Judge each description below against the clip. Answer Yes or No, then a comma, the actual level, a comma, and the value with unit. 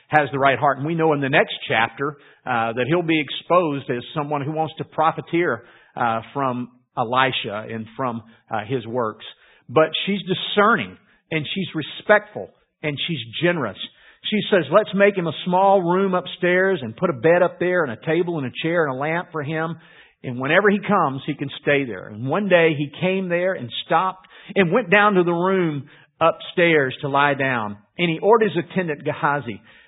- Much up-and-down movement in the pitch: No, average, 4.7 semitones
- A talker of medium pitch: Yes, medium, 160 Hz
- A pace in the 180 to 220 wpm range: Yes, average, 195 wpm